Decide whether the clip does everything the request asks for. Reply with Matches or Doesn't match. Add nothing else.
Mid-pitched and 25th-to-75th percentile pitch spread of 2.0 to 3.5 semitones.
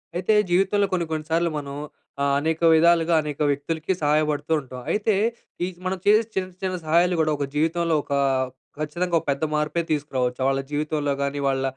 Matches